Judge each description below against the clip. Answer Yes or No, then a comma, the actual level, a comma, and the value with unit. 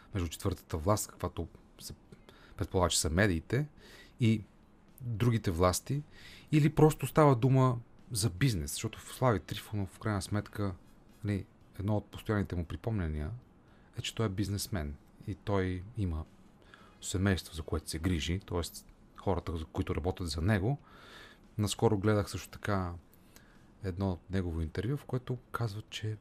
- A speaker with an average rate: Yes, average, 140 wpm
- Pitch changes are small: No, average, 3.6 semitones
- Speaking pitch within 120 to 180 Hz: No, low, 100 Hz